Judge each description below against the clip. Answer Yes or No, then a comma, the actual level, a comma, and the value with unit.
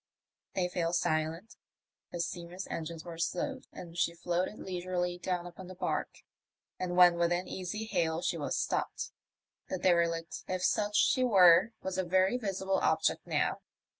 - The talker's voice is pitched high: No, medium, 180 Hz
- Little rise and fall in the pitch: Yes, narrow, 1.7 semitones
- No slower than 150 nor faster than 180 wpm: Yes, average, 155 wpm